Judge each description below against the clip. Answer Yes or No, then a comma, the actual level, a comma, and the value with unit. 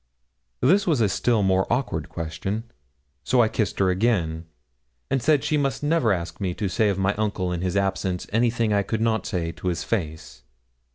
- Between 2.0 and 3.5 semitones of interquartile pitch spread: No, average, 4.5 semitones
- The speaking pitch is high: No, low, 100 Hz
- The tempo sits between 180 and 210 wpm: Yes, average, 190 wpm